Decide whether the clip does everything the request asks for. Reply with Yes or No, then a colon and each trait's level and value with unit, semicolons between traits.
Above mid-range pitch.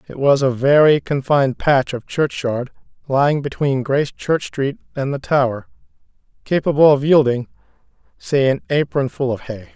No: low, 135 Hz